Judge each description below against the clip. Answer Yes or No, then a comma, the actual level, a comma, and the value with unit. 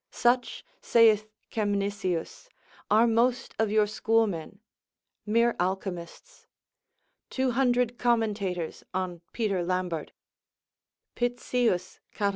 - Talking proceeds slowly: Yes, slow, 85 wpm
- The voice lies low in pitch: No, high, 215 Hz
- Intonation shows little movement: No, average, 4.3 semitones